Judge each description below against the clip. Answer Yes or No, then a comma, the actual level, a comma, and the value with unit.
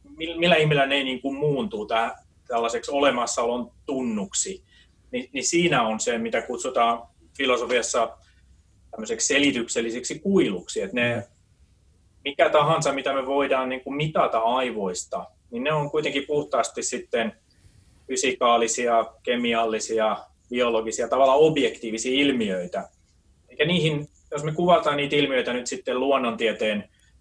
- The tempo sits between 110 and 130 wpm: Yes, average, 115 wpm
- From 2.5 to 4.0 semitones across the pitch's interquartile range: No, average, 4.7 semitones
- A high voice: No, low, 125 Hz